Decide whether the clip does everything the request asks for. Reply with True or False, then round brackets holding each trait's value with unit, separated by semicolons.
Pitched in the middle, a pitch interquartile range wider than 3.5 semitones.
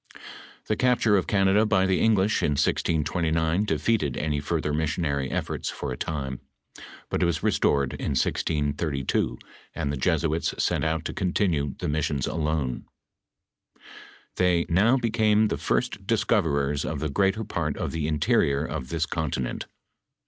False (80 Hz; 4.7 semitones)